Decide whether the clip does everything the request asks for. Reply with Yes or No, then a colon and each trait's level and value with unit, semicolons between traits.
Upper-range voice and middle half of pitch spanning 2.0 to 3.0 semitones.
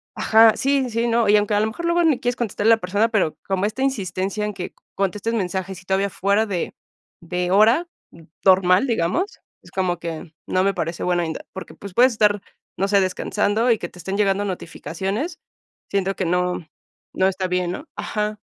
No: high, 200 Hz; average, 3.5 semitones